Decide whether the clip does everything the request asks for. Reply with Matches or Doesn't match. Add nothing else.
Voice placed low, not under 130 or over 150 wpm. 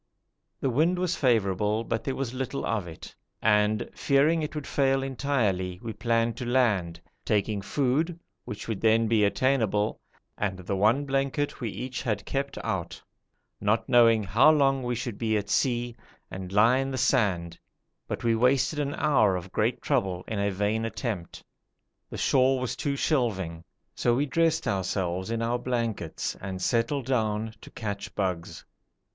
Doesn't match